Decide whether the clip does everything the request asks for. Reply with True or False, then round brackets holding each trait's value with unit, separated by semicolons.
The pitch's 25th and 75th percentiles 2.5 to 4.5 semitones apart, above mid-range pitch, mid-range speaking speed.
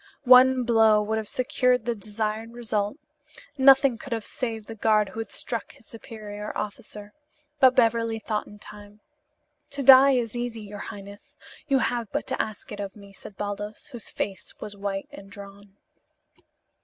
True (2.8 semitones; 220 Hz; 170 wpm)